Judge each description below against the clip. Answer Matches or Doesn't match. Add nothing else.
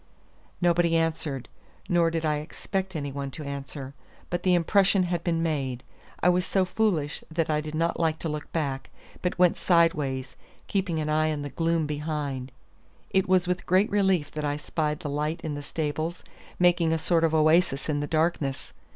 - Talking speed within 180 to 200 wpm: Matches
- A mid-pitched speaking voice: Matches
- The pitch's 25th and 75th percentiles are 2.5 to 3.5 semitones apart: Matches